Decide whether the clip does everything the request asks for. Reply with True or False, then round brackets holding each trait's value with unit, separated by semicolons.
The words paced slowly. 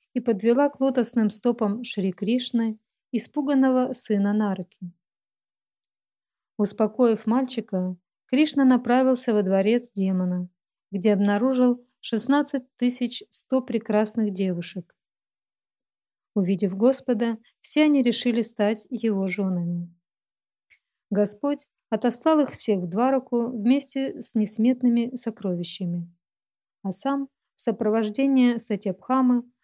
True (95 wpm)